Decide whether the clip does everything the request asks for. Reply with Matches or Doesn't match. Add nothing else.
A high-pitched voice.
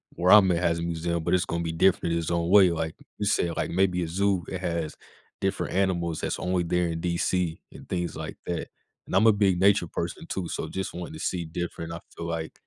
Doesn't match